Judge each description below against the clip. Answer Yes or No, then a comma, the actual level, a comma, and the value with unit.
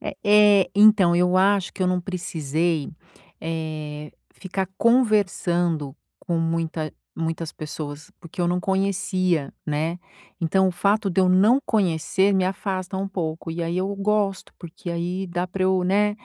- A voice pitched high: No, medium, 180 Hz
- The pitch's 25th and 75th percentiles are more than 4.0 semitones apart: No, average, 2.9 semitones